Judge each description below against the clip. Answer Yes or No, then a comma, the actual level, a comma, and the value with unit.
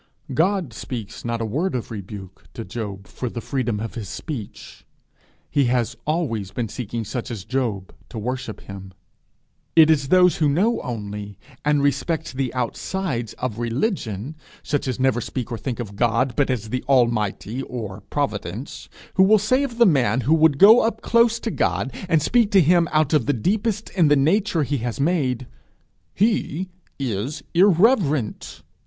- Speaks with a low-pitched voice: Yes, low, 130 Hz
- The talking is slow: No, average, 170 wpm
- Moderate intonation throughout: No, wide, 6.4 semitones